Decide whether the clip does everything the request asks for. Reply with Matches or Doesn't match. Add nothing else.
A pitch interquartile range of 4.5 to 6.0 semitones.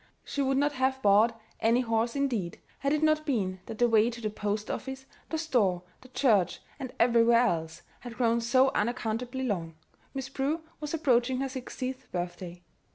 Doesn't match